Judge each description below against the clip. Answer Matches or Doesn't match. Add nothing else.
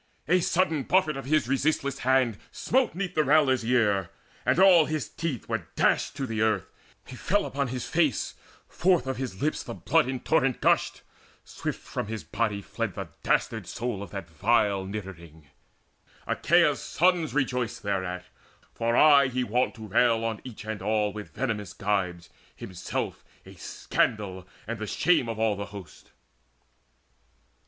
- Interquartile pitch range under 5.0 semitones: Doesn't match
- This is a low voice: Matches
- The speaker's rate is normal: Matches